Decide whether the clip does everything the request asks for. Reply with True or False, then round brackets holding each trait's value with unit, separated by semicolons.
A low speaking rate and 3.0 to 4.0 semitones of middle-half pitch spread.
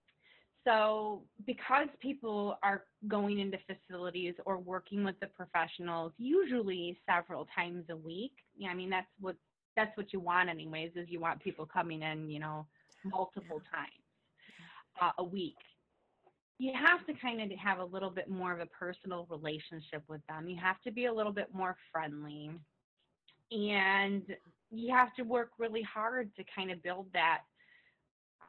False (160 wpm; 3.7 semitones)